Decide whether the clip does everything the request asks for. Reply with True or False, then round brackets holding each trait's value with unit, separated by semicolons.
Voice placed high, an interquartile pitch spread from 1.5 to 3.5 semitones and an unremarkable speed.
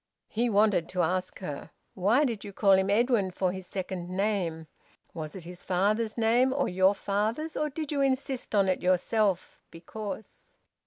False (200 Hz; 3.9 semitones; 170 wpm)